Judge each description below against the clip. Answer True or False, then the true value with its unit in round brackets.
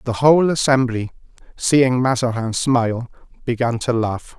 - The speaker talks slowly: True (125 wpm)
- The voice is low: True (125 Hz)